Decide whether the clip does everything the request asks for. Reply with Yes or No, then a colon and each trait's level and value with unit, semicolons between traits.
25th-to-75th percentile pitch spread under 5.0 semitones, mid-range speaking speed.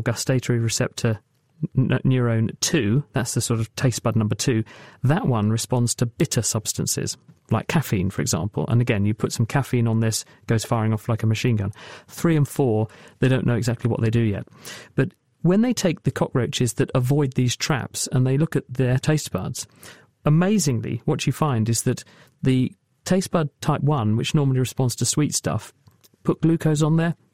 Yes: average, 4.1 semitones; average, 190 wpm